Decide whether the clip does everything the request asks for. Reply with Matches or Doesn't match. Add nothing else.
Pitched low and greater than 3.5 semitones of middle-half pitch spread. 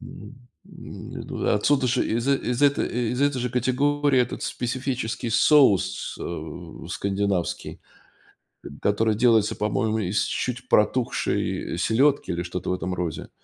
Matches